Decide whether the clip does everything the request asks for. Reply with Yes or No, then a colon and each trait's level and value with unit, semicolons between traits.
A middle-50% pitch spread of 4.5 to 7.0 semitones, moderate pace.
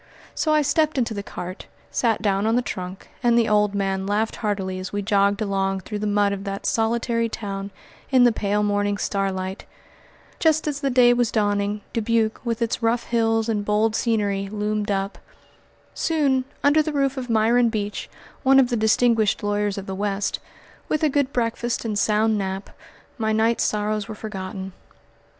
No: average, 2.8 semitones; average, 180 wpm